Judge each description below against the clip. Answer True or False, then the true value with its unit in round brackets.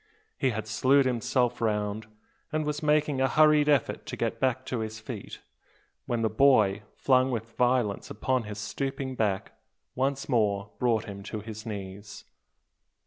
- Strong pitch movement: False (3.9 semitones)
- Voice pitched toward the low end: True (115 Hz)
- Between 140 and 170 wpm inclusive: True (150 wpm)